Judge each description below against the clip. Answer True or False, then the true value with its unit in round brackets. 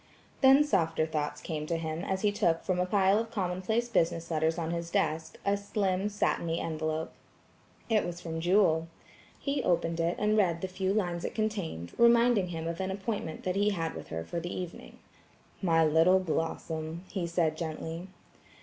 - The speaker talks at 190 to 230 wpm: False (180 wpm)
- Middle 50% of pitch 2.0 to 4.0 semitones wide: True (3.5 semitones)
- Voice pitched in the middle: True (175 Hz)